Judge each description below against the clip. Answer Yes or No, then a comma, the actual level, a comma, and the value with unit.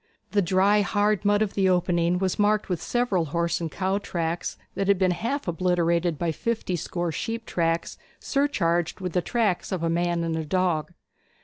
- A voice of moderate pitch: Yes, medium, 180 Hz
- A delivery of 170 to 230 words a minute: Yes, average, 185 wpm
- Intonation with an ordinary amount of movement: Yes, average, 3.2 semitones